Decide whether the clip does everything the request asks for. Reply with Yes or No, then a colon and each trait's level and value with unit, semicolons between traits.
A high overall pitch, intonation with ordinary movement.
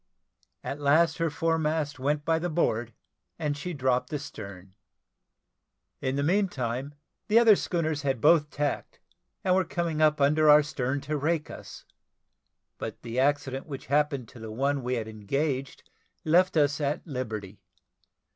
No: medium, 145 Hz; average, 3.3 semitones